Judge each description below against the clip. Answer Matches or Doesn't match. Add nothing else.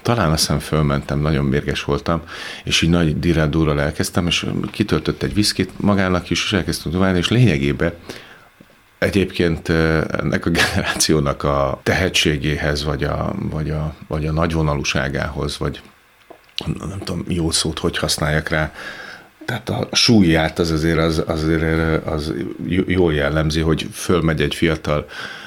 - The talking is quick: Doesn't match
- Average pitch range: Doesn't match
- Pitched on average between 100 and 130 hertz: Doesn't match